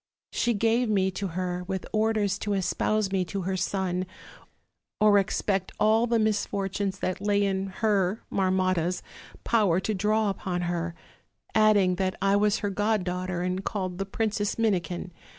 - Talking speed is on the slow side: No, average, 165 wpm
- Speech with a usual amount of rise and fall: No, narrow, 2.3 semitones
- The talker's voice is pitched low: No, high, 195 Hz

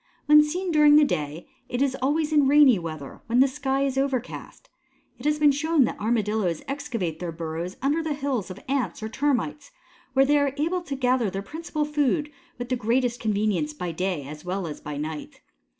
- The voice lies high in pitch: Yes, very high, 260 Hz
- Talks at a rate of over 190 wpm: Yes, average, 200 wpm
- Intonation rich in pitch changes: Yes, wide, 7.8 semitones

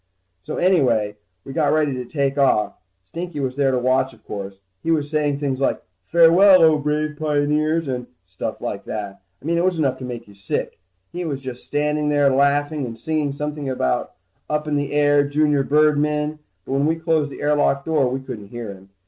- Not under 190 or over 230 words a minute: Yes, average, 200 wpm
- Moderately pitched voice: Yes, medium, 145 Hz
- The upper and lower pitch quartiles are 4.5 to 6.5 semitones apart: No, average, 2.8 semitones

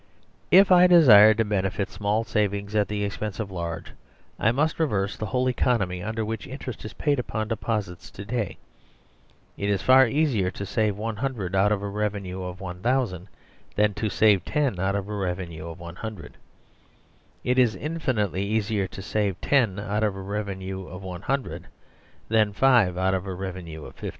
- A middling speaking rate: Yes, average, 175 wpm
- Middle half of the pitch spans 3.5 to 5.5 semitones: No, average, 3.0 semitones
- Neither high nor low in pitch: No, low, 105 Hz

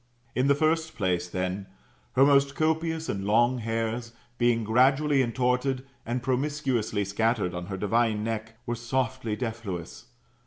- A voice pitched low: Yes, low, 120 Hz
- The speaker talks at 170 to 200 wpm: No, average, 140 wpm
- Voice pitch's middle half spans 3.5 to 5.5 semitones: Yes, average, 3.9 semitones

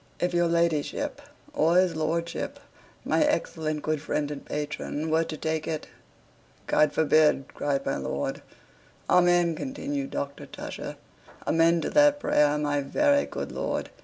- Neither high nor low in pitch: Yes, medium, 160 Hz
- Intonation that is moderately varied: Yes, average, 3.0 semitones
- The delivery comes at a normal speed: Yes, average, 145 wpm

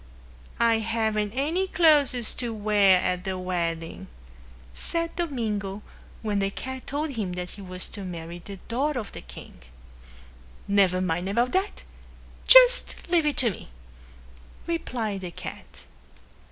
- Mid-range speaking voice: No, high, 215 Hz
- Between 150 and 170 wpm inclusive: No, average, 140 wpm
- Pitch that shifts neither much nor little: No, wide, 6.6 semitones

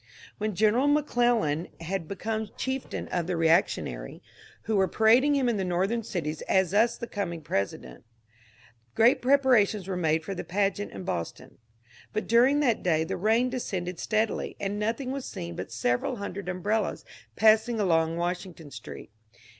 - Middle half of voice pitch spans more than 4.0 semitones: Yes, average, 5.2 semitones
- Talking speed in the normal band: Yes, average, 155 wpm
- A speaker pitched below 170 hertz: No, high, 200 Hz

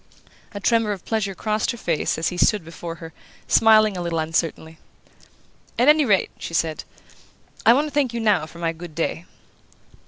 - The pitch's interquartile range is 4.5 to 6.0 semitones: Yes, average, 5.2 semitones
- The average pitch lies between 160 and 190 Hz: Yes, medium, 185 Hz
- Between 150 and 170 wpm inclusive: No, average, 185 wpm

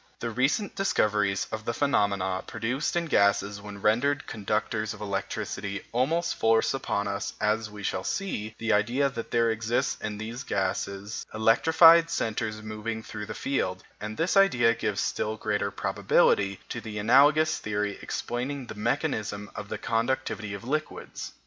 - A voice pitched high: No, low, 110 Hz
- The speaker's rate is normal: Yes, average, 155 wpm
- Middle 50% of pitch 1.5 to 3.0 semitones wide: No, average, 3.9 semitones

